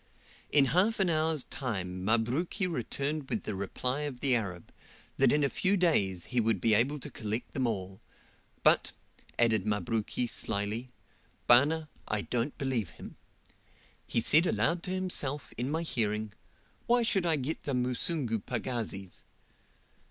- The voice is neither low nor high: No, low, 125 Hz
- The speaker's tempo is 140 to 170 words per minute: Yes, average, 150 wpm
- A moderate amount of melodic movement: No, wide, 6.2 semitones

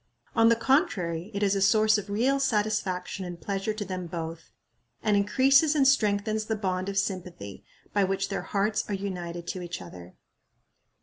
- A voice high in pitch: Yes, high, 200 Hz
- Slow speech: No, average, 175 wpm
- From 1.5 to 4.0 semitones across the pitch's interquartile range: Yes, average, 3.0 semitones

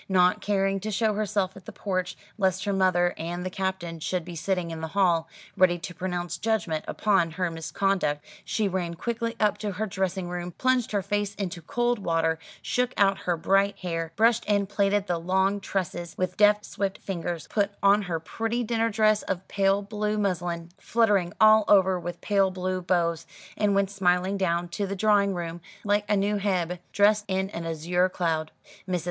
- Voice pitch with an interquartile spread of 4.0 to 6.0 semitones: No, average, 2.8 semitones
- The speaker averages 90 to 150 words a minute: No, average, 190 wpm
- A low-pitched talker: No, high, 190 Hz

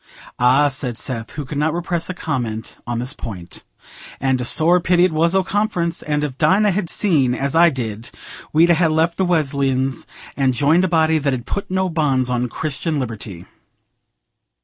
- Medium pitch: Yes, medium, 150 Hz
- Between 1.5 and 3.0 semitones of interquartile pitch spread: No, average, 5.0 semitones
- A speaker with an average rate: Yes, average, 190 wpm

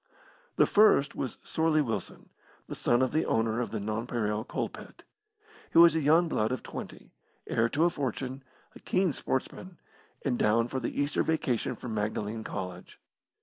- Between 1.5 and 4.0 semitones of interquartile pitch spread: No, wide, 5.6 semitones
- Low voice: Yes, low, 125 Hz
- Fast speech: No, average, 165 wpm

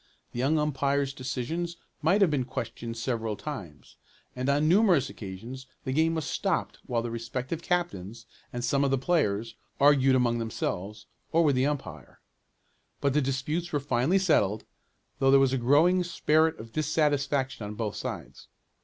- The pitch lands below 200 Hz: Yes, low, 135 Hz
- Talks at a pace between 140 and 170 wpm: Yes, average, 160 wpm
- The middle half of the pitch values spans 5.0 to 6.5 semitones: No, average, 4.5 semitones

